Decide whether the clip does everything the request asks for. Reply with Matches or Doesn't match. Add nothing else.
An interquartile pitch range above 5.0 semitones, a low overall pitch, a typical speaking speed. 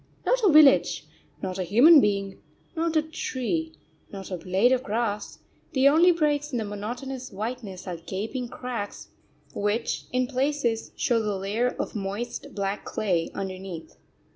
Doesn't match